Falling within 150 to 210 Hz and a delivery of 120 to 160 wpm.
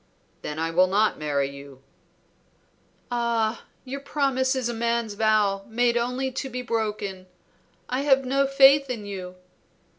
No: high, 235 Hz; average, 145 wpm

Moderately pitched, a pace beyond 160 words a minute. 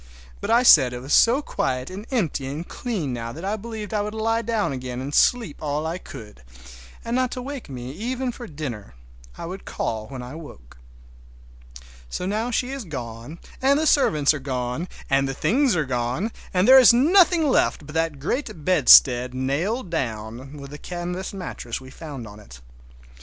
Yes: medium, 155 Hz; average, 185 wpm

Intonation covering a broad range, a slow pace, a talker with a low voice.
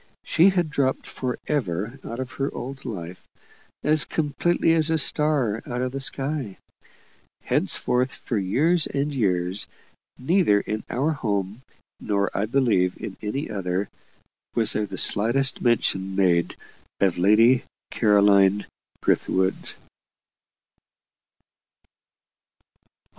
Yes: wide, 5.7 semitones; slow, 115 wpm; low, 120 Hz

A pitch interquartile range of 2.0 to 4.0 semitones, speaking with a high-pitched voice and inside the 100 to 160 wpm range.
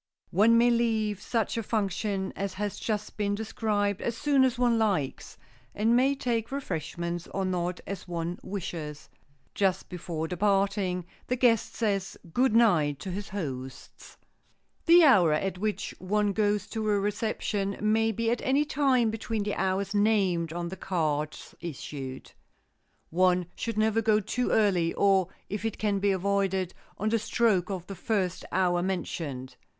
Yes: average, 3.6 semitones; high, 200 Hz; average, 155 wpm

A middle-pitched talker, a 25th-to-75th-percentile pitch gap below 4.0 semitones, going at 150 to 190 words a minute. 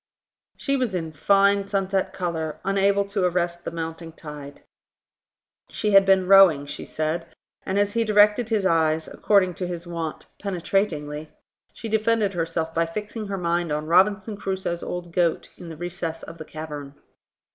Yes: medium, 180 Hz; average, 3.5 semitones; average, 160 wpm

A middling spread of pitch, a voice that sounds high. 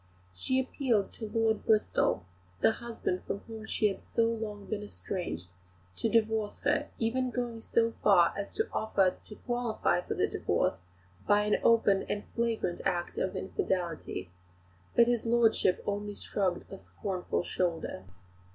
Yes: average, 3.4 semitones; high, 210 Hz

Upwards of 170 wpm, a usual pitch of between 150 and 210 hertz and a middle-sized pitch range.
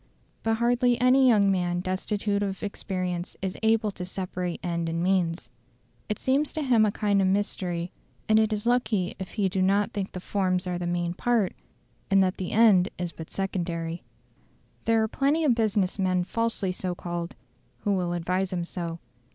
Yes: average, 185 wpm; high, 190 Hz; average, 3.5 semitones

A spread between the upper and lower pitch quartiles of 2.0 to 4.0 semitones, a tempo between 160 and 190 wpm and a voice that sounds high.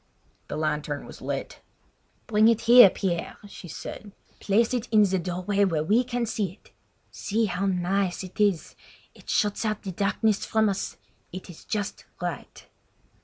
Yes: average, 3.1 semitones; average, 165 wpm; high, 200 Hz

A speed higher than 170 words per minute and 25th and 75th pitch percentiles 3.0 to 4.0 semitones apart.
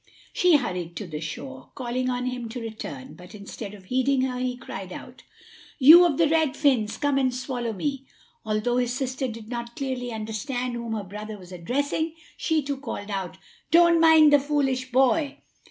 No: average, 185 wpm; average, 4.5 semitones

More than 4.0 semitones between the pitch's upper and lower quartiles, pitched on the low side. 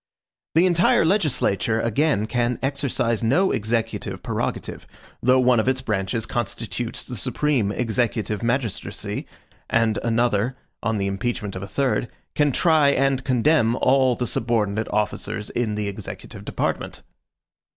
No: average, 3.4 semitones; low, 120 Hz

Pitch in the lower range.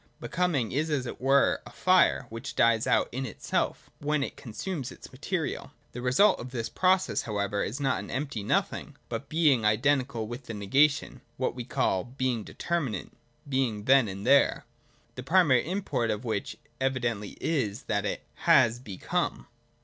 Yes: low, 130 Hz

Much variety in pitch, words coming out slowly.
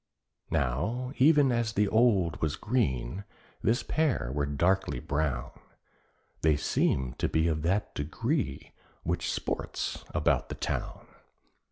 Yes: wide, 8.5 semitones; slow, 125 wpm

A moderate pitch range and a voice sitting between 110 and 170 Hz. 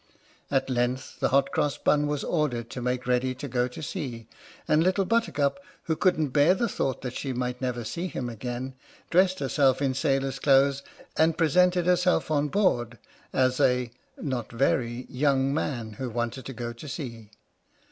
Yes: average, 3.5 semitones; low, 135 Hz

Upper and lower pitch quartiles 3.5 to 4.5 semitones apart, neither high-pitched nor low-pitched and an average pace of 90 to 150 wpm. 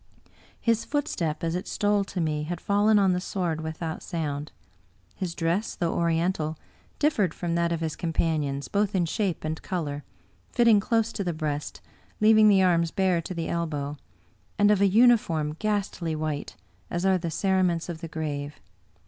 No: average, 4.0 semitones; medium, 170 Hz; average, 175 wpm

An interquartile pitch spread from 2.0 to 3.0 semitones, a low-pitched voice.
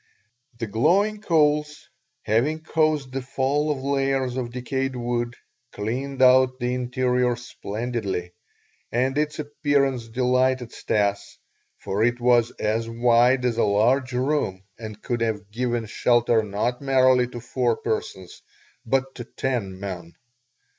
Yes: average, 2.7 semitones; low, 125 Hz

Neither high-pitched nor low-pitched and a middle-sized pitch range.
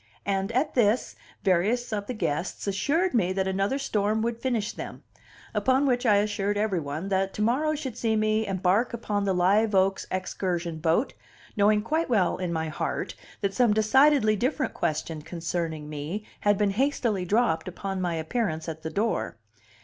No: high, 205 Hz; average, 4.3 semitones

